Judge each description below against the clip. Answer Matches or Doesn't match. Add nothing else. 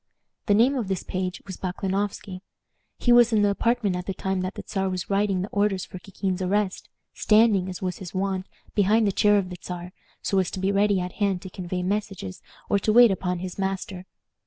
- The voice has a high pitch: Matches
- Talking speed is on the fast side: Matches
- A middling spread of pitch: Doesn't match